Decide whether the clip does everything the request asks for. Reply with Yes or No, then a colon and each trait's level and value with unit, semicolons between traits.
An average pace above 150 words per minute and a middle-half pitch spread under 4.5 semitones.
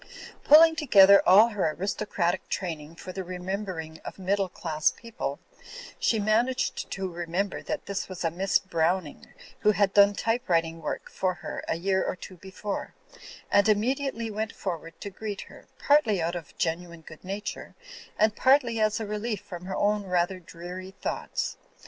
Yes: average, 165 wpm; average, 3.3 semitones